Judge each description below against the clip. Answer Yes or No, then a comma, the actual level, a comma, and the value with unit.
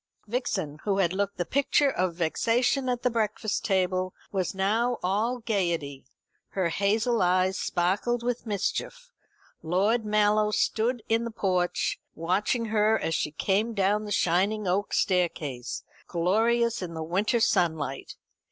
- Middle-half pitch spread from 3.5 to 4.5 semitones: Yes, average, 4.1 semitones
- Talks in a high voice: Yes, high, 200 Hz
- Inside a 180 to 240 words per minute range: No, average, 140 wpm